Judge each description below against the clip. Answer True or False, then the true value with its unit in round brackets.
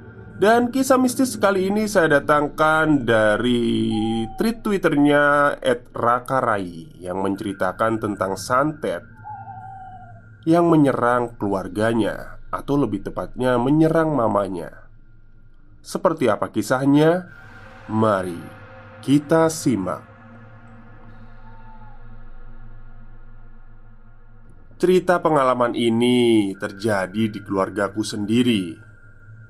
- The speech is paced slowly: True (75 wpm)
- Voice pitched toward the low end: True (115 Hz)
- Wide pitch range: False (4.8 semitones)